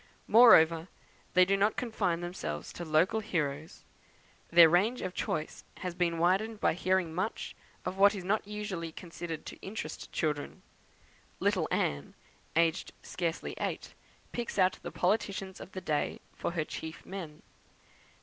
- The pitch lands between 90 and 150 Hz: No, medium, 180 Hz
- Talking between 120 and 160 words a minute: Yes, average, 145 wpm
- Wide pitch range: No, average, 3.3 semitones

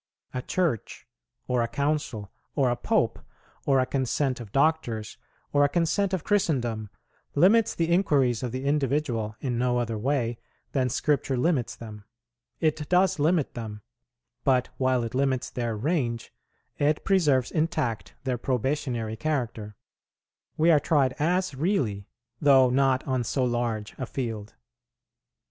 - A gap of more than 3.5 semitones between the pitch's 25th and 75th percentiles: Yes, average, 4.3 semitones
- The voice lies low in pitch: Yes, low, 130 Hz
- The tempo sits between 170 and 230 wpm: No, average, 140 wpm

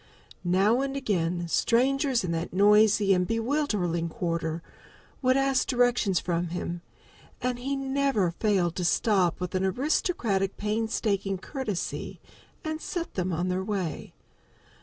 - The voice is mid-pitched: No, high, 205 Hz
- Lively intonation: Yes, wide, 6.1 semitones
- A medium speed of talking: No, slow, 130 wpm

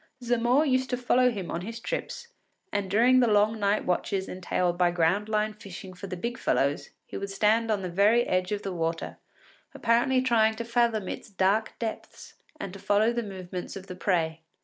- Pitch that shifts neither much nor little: Yes, average, 4.1 semitones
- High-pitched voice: Yes, high, 210 Hz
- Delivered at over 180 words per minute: Yes, average, 195 wpm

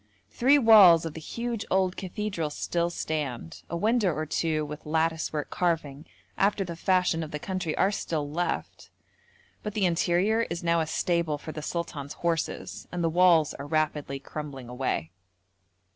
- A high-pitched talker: No, medium, 165 Hz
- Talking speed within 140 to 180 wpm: Yes, average, 165 wpm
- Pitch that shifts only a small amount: No, average, 3.3 semitones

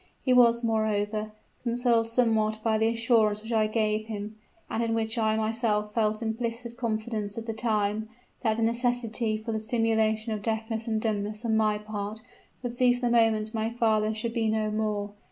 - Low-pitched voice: No, high, 220 Hz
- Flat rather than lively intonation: Yes, narrow, 1.2 semitones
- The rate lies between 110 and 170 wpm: No, average, 180 wpm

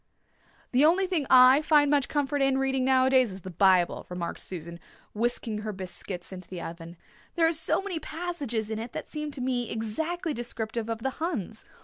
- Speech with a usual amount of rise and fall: No, wide, 6.0 semitones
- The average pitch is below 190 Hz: No, very high, 250 Hz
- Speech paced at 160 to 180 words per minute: No, average, 195 wpm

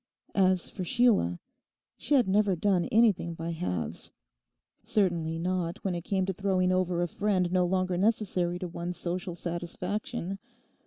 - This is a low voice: No, medium, 185 Hz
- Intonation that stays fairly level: Yes, narrow, 2.2 semitones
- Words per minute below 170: Yes, average, 150 wpm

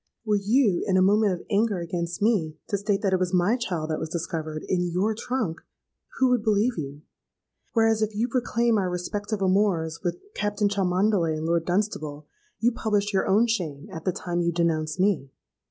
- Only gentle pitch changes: No, average, 3.9 semitones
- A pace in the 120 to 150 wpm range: No, average, 190 wpm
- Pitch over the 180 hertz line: Yes, high, 190 Hz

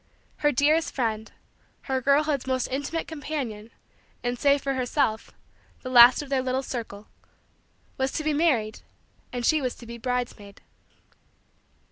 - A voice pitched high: Yes, very high, 260 Hz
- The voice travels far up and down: No, average, 3.3 semitones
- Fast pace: No, average, 140 wpm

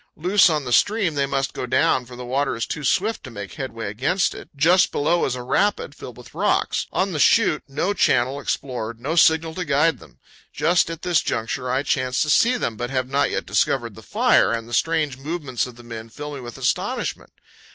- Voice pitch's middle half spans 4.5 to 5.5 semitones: Yes, average, 5.0 semitones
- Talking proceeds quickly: Yes, fast, 220 wpm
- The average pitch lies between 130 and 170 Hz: Yes, medium, 140 Hz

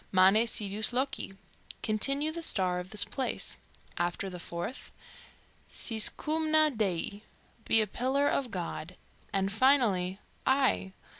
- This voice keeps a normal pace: No, slow, 125 wpm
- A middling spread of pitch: No, wide, 6.3 semitones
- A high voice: Yes, high, 215 Hz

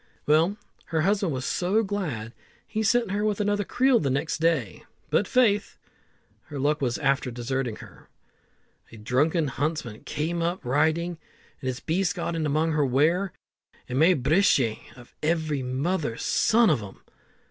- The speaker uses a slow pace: No, average, 160 wpm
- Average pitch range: No, wide, 5.8 semitones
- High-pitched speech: No, medium, 155 Hz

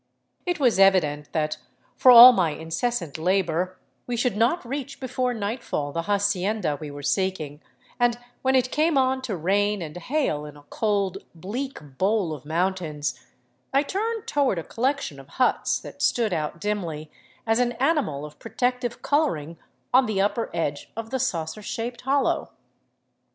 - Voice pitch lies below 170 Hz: No, high, 205 Hz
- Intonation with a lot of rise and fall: Yes, wide, 7.6 semitones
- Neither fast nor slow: Yes, average, 160 wpm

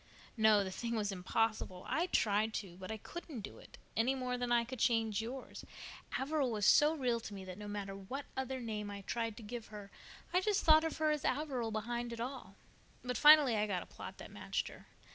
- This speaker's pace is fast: Yes, fast, 220 wpm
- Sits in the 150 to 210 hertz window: No, high, 230 Hz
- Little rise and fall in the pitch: No, average, 4.1 semitones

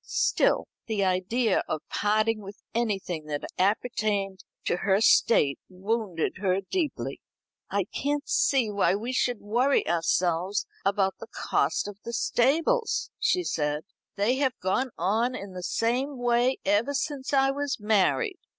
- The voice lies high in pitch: Yes, high, 215 Hz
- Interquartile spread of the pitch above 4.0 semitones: Yes, average, 5.2 semitones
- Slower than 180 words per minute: Yes, average, 140 wpm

